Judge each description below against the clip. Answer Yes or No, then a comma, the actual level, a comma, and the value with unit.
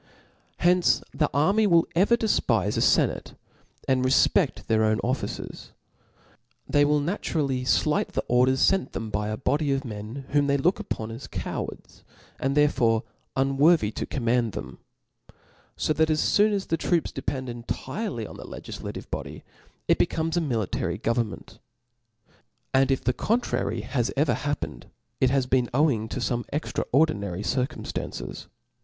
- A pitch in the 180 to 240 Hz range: No, low, 135 Hz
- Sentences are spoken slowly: No, average, 155 wpm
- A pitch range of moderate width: Yes, average, 4.7 semitones